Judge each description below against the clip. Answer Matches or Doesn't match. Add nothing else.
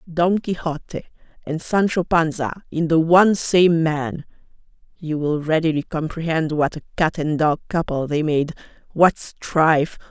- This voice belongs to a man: Doesn't match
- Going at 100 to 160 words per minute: Matches